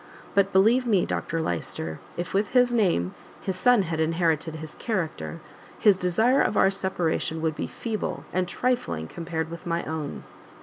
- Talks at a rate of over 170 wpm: No, average, 165 wpm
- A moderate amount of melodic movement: Yes, average, 4.3 semitones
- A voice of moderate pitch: Yes, medium, 175 Hz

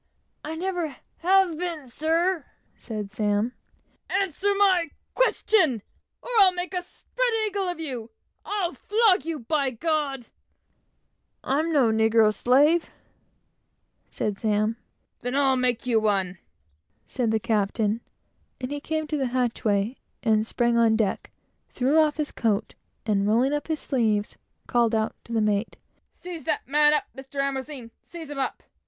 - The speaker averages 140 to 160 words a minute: Yes, average, 150 wpm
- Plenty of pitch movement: Yes, wide, 6.4 semitones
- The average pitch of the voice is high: Yes, very high, 270 Hz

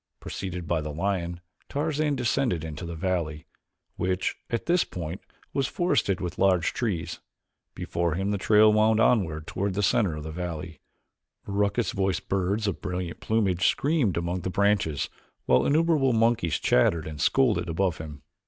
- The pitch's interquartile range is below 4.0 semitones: No, average, 4.6 semitones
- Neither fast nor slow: Yes, average, 155 wpm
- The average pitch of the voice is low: Yes, very low, 95 Hz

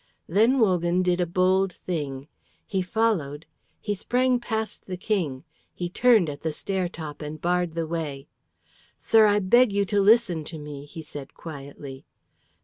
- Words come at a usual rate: Yes, average, 160 wpm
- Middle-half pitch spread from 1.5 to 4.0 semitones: No, average, 5.1 semitones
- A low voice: No, medium, 180 Hz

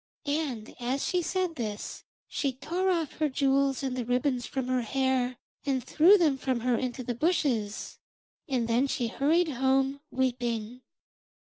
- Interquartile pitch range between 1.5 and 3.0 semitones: Yes, average, 2.7 semitones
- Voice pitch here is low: No, very high, 265 Hz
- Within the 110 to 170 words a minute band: Yes, average, 155 wpm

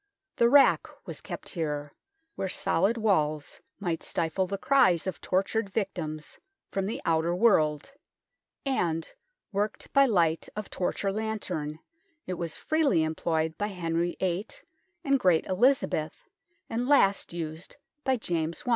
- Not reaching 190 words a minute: Yes, average, 140 wpm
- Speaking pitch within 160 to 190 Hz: Yes, medium, 185 Hz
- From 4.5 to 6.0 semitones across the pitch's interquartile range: Yes, average, 5.2 semitones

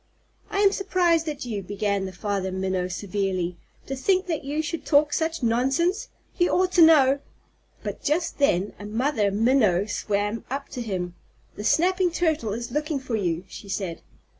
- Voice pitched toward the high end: Yes, very high, 250 Hz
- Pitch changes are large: Yes, wide, 8.0 semitones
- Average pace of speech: Yes, average, 175 wpm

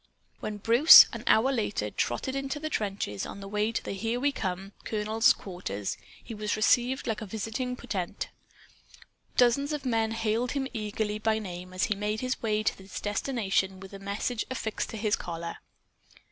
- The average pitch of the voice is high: Yes, high, 215 Hz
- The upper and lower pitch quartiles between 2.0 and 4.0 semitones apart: Yes, average, 3.5 semitones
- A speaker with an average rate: Yes, average, 180 wpm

